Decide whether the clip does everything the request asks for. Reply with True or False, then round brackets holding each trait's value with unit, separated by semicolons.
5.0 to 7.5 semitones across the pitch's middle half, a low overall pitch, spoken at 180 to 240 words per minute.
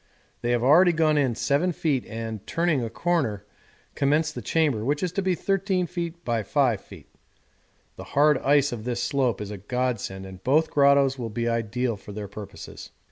True (5.6 semitones; 130 Hz; 190 wpm)